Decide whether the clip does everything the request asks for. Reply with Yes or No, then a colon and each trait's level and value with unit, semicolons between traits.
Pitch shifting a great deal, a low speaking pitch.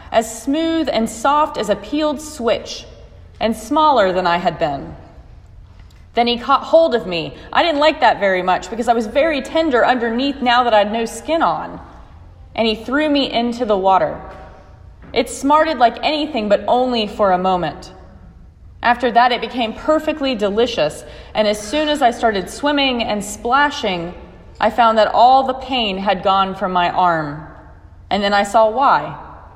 No: wide, 6.1 semitones; high, 225 Hz